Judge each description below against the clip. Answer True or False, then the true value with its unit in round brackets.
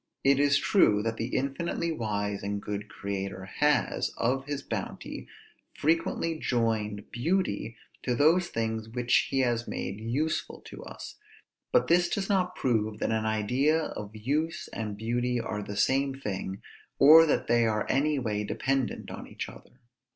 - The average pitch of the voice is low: True (120 Hz)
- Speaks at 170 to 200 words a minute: False (160 wpm)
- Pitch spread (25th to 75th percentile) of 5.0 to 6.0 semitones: True (5.3 semitones)